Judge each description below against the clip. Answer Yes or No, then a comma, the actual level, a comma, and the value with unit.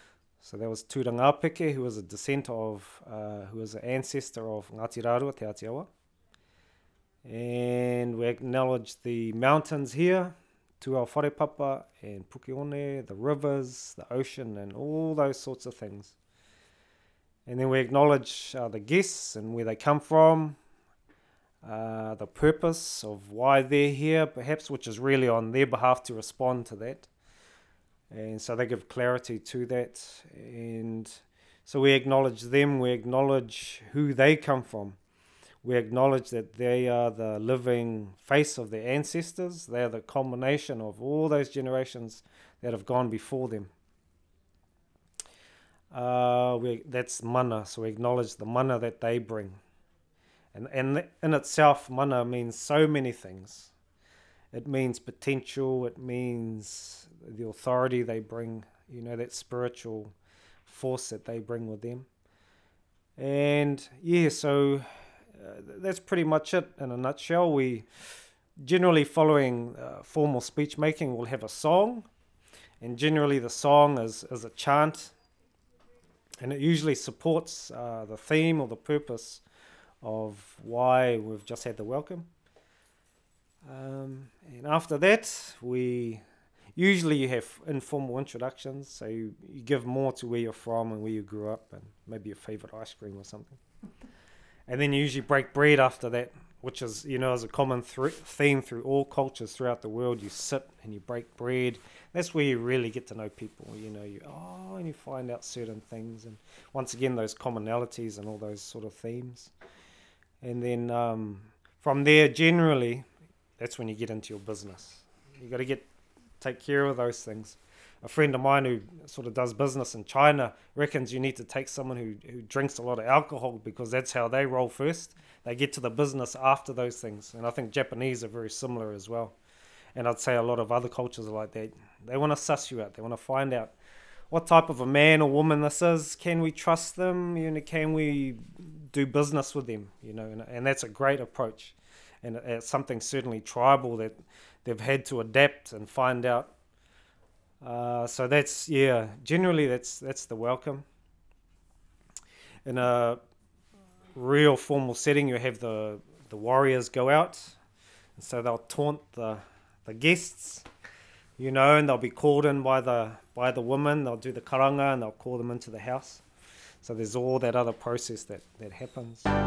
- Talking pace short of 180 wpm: Yes, average, 170 wpm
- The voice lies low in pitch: Yes, low, 125 Hz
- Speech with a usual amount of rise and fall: Yes, average, 4.0 semitones